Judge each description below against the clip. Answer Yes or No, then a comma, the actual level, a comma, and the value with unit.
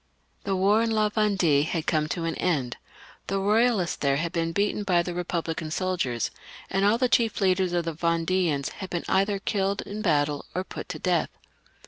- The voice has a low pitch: No, medium, 180 Hz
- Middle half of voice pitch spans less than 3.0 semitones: No, average, 3.3 semitones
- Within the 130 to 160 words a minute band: No, average, 195 wpm